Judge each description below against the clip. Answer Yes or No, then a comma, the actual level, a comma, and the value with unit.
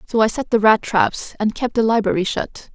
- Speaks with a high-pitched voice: Yes, high, 220 Hz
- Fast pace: Yes, fast, 240 wpm